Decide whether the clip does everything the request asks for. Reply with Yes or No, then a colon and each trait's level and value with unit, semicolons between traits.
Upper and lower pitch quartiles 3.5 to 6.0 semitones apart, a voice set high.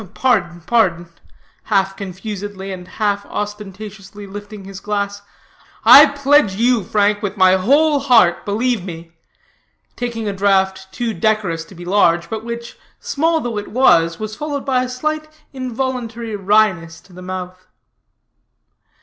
Yes: average, 3.9 semitones; high, 205 Hz